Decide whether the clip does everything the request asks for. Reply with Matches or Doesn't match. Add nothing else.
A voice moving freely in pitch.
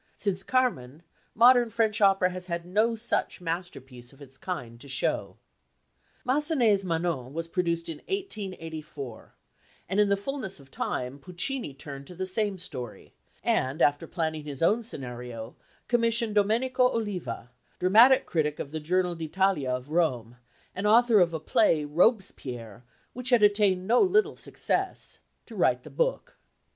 Matches